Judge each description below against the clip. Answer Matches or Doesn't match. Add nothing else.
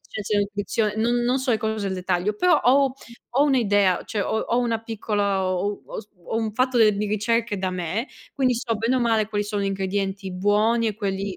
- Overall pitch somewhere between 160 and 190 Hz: Doesn't match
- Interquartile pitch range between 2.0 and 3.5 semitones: Matches